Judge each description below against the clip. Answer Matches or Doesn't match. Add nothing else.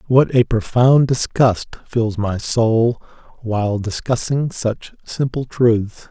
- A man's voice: Matches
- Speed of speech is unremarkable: Doesn't match